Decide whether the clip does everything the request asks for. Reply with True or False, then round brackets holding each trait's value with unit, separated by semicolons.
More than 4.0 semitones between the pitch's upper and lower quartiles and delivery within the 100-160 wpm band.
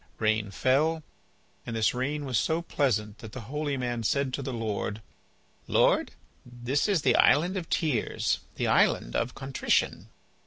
True (4.6 semitones; 155 wpm)